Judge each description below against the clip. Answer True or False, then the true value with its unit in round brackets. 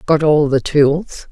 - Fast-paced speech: False (185 wpm)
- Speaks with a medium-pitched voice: True (150 Hz)